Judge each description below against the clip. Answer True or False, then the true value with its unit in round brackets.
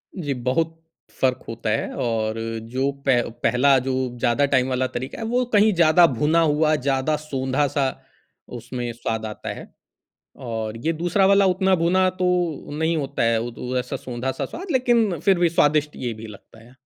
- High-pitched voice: False (140 Hz)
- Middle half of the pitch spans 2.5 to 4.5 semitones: False (5.5 semitones)